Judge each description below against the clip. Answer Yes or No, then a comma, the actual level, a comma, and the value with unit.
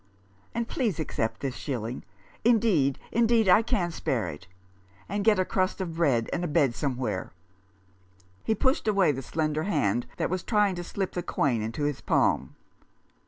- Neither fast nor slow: Yes, average, 175 wpm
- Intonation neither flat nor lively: No, wide, 7.9 semitones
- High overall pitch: No, medium, 165 Hz